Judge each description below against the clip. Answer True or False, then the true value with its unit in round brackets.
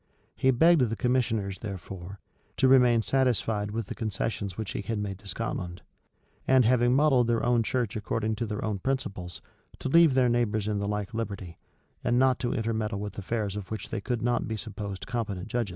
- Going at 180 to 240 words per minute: True (200 wpm)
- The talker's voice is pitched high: False (110 Hz)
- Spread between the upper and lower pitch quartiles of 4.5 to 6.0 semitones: False (3.2 semitones)